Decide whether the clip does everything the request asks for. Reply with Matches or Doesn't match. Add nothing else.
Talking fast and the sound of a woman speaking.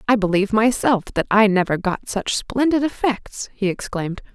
Doesn't match